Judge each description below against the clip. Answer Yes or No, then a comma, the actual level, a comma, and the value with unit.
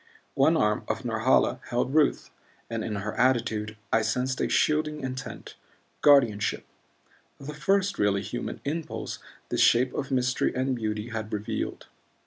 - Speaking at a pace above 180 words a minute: No, average, 140 wpm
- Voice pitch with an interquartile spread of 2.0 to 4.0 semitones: No, average, 4.5 semitones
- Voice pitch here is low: Yes, low, 125 Hz